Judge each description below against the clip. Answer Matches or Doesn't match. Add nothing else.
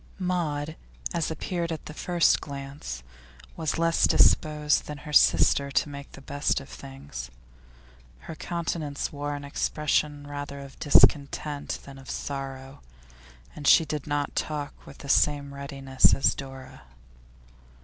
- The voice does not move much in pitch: Matches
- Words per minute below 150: Matches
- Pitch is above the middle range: Doesn't match